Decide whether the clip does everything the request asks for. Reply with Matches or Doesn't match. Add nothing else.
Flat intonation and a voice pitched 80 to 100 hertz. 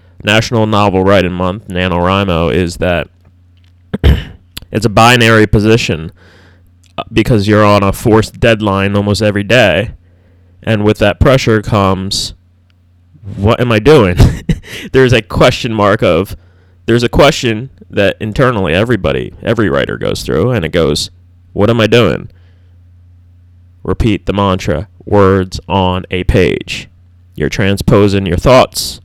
Doesn't match